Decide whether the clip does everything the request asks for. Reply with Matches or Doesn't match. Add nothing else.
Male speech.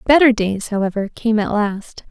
Doesn't match